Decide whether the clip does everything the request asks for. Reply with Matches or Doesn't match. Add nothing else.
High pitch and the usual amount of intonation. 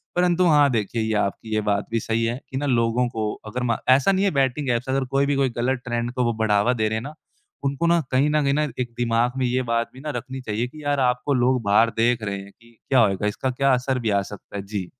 Doesn't match